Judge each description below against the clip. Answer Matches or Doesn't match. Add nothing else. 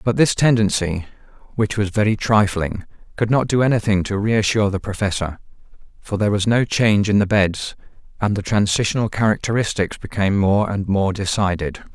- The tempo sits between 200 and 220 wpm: Doesn't match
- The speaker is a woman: Doesn't match